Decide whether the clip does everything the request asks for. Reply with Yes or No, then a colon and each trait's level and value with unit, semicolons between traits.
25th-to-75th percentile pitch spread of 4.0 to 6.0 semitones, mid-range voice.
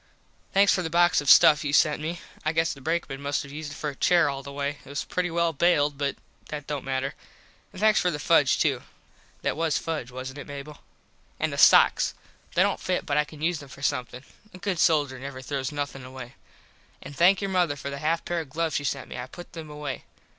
No: average, 2.9 semitones; medium, 150 Hz